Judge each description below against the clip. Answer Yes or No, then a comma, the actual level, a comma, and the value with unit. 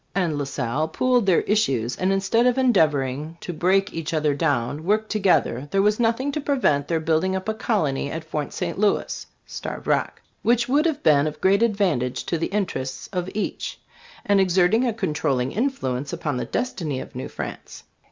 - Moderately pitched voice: Yes, medium, 180 Hz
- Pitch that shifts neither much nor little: No, wide, 6.5 semitones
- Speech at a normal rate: Yes, average, 190 wpm